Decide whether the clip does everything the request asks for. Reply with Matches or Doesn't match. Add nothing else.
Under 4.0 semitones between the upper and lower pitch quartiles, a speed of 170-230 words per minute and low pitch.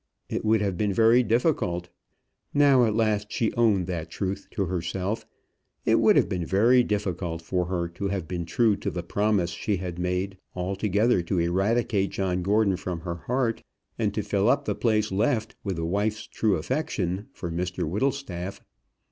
Matches